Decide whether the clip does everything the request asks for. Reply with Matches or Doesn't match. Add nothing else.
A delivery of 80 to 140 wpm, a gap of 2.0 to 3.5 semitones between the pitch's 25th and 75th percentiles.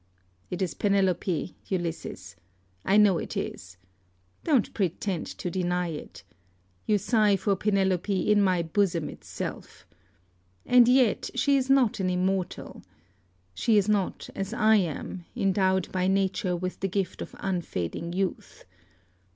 Matches